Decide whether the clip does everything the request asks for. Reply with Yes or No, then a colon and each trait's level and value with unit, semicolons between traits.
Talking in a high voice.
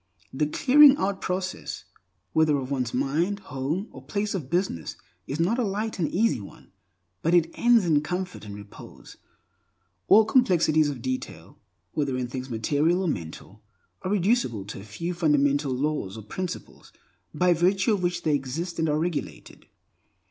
No: medium, 160 Hz